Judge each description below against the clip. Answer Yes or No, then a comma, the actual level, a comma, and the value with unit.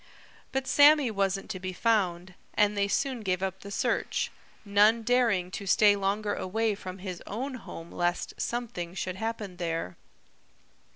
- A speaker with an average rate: Yes, average, 155 wpm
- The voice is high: Yes, high, 200 Hz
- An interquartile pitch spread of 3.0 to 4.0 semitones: Yes, average, 3.5 semitones